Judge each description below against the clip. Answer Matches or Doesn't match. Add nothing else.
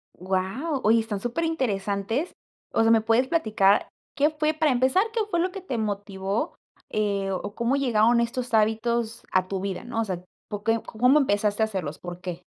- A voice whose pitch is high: Matches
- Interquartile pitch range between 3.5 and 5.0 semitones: Matches